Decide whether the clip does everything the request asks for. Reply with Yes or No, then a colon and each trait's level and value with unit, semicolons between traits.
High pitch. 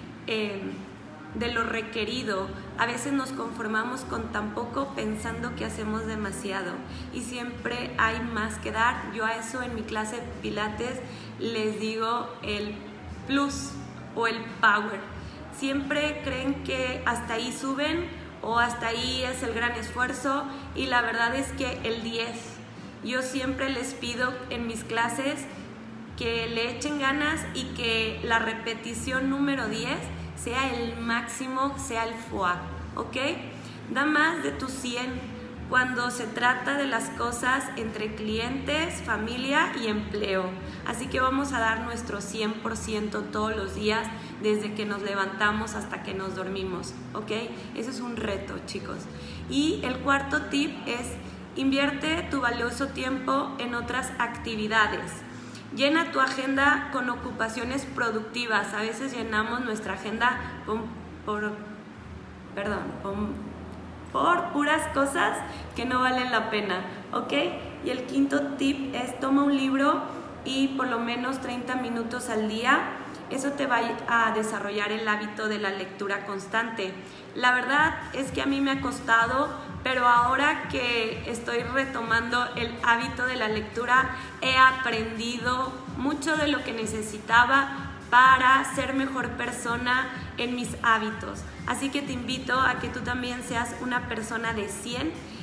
Yes: high, 240 Hz